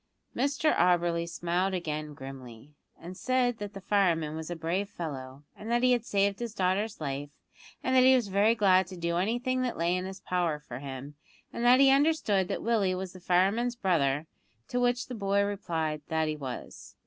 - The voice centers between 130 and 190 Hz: Yes, medium, 185 Hz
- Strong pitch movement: Yes, wide, 6.2 semitones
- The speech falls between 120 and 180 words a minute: No, average, 195 wpm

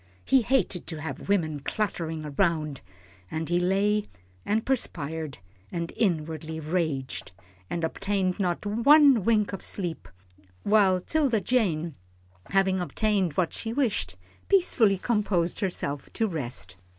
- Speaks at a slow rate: Yes, slow, 125 wpm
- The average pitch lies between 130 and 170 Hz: No, medium, 185 Hz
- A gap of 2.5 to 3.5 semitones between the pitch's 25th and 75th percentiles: No, average, 4.9 semitones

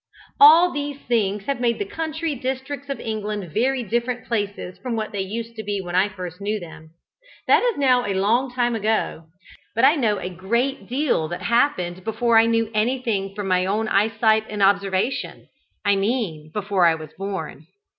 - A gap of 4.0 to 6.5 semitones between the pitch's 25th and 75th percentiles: Yes, average, 4.3 semitones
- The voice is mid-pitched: No, high, 215 Hz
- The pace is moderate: Yes, average, 185 wpm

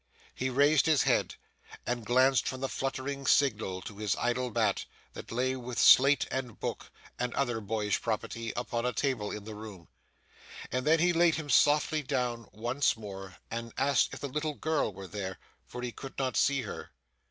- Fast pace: No, average, 185 wpm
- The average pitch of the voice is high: No, low, 125 Hz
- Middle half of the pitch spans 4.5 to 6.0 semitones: No, average, 3.9 semitones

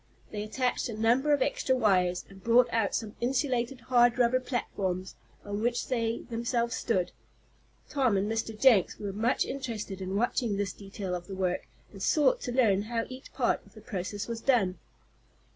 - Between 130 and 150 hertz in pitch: No, high, 225 Hz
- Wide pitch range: No, average, 3.8 semitones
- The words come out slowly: No, average, 175 wpm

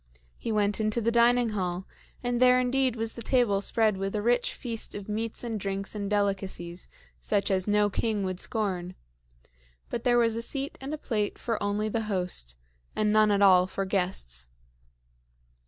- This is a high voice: Yes, high, 210 Hz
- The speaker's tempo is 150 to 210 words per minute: Yes, average, 180 wpm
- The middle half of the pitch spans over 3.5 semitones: No, average, 3.1 semitones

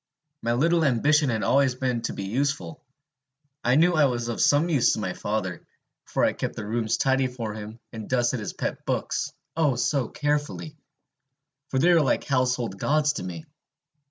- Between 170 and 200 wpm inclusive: Yes, average, 185 wpm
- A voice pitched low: Yes, low, 130 Hz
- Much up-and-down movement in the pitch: No, average, 4.5 semitones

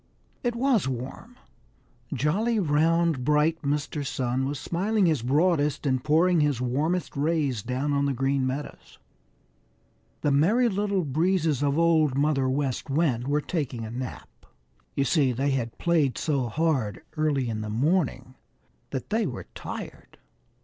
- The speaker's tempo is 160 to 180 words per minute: No, average, 145 wpm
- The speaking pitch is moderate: Yes, medium, 145 Hz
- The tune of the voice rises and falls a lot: No, average, 4.2 semitones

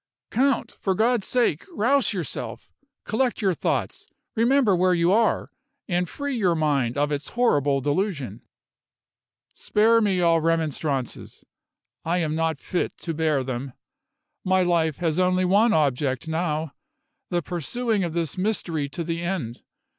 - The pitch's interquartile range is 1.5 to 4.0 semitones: No, average, 5.1 semitones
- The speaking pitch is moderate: Yes, medium, 175 Hz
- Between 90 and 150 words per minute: Yes, average, 140 wpm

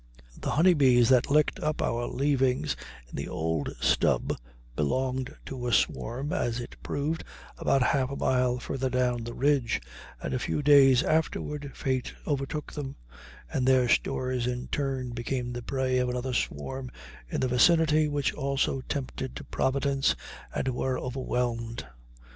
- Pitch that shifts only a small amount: Yes, narrow, 2.1 semitones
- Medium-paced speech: Yes, average, 150 wpm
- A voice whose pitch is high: No, low, 130 Hz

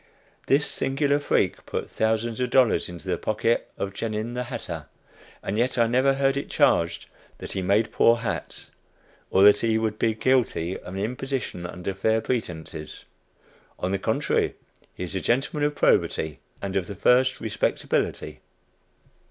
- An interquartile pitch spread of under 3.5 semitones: No, average, 4.8 semitones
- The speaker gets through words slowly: No, average, 160 wpm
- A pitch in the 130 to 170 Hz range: No, low, 110 Hz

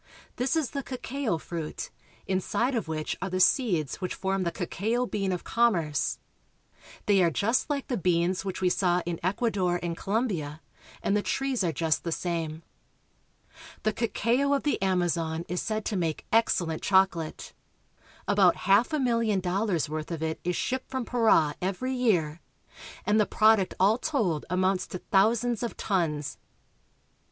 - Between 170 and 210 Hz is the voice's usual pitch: Yes, high, 190 Hz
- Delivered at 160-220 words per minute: Yes, average, 165 wpm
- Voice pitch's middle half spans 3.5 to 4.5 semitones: No, average, 5.2 semitones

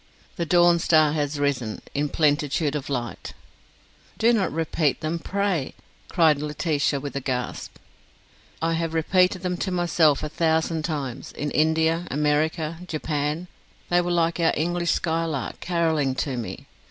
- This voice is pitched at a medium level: Yes, medium, 160 Hz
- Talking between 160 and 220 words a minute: No, average, 150 wpm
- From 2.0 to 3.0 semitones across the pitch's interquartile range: Yes, narrow, 2.6 semitones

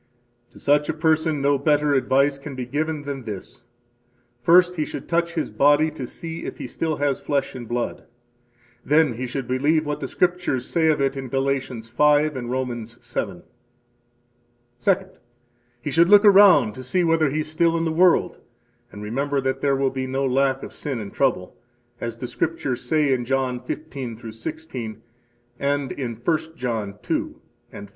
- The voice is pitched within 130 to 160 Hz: Yes, medium, 140 Hz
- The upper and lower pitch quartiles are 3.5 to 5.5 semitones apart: Yes, average, 3.9 semitones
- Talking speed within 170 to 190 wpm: Yes, average, 180 wpm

